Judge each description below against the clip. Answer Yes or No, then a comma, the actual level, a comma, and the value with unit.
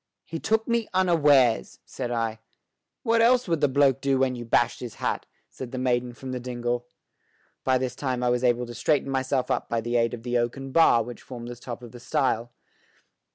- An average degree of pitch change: No, narrow, 2.3 semitones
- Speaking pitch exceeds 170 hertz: No, low, 125 Hz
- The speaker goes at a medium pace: No, fast, 210 wpm